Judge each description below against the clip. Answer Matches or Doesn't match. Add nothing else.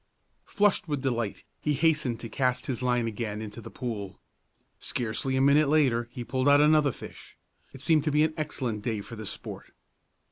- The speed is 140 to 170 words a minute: Doesn't match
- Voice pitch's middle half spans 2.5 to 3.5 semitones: Doesn't match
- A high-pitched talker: Doesn't match